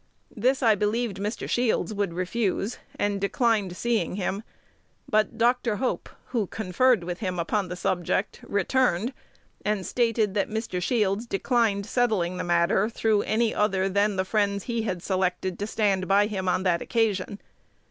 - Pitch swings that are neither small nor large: Yes, average, 3.3 semitones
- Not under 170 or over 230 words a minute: No, average, 160 wpm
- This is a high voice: Yes, high, 205 Hz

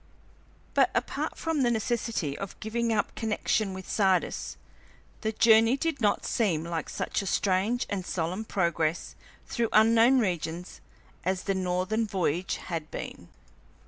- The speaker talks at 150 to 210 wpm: No, average, 140 wpm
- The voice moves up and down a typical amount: Yes, average, 4.1 semitones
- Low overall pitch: No, high, 200 Hz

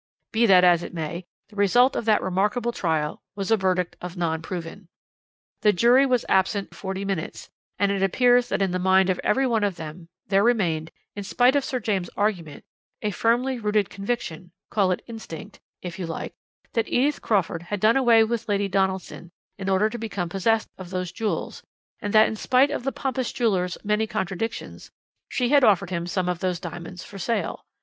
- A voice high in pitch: Yes, high, 200 Hz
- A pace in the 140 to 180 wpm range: No, average, 195 wpm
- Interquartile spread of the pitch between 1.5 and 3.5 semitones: No, average, 4.0 semitones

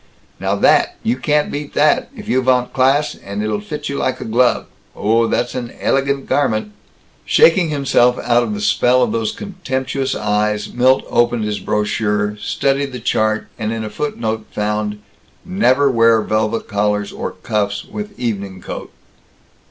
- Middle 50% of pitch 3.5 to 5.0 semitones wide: Yes, average, 4.4 semitones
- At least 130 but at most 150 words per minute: No, average, 160 wpm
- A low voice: Yes, low, 120 Hz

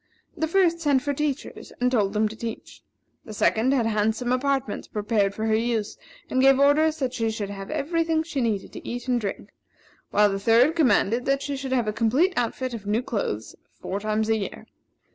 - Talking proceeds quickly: Yes, fast, 210 wpm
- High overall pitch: Yes, high, 240 Hz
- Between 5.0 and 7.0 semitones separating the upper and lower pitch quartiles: No, average, 4.3 semitones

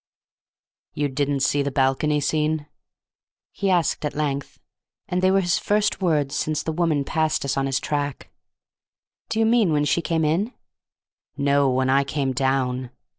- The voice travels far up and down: No, average, 3.3 semitones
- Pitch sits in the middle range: Yes, medium, 145 Hz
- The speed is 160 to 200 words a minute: Yes, average, 165 wpm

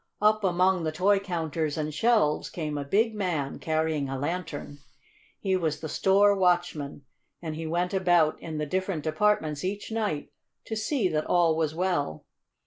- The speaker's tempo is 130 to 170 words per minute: Yes, average, 165 wpm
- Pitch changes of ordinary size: Yes, average, 3.8 semitones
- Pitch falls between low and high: Yes, medium, 170 Hz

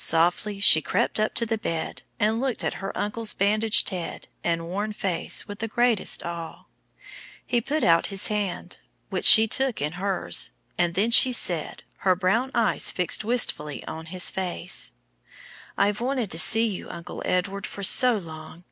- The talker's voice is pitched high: Yes, high, 200 Hz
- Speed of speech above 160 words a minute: Yes, average, 170 wpm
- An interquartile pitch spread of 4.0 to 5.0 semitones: Yes, average, 4.4 semitones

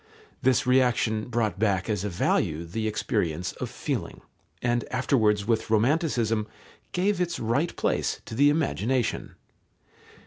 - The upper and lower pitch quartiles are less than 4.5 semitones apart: Yes, average, 3.7 semitones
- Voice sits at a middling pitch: No, low, 115 Hz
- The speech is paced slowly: Yes, slow, 130 wpm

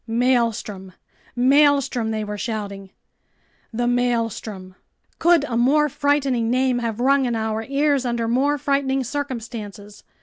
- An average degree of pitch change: Yes, average, 3.8 semitones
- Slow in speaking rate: Yes, slow, 125 wpm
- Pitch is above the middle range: Yes, high, 245 Hz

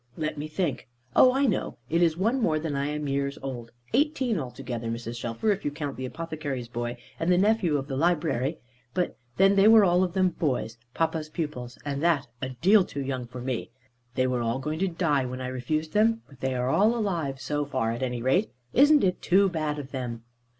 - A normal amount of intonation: No, wide, 5.7 semitones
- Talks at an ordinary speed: No, fast, 215 wpm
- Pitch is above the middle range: No, medium, 150 Hz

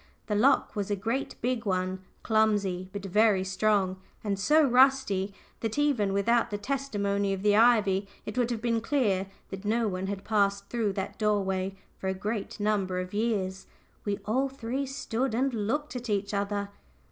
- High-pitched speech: Yes, high, 210 Hz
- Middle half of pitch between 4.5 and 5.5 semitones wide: No, average, 3.2 semitones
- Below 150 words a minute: No, average, 175 wpm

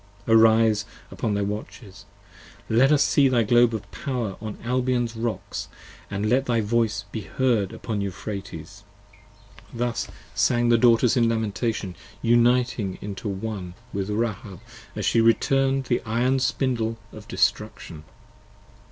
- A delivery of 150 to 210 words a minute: No, slow, 135 wpm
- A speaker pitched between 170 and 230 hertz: No, low, 115 Hz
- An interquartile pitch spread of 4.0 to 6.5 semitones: No, average, 2.8 semitones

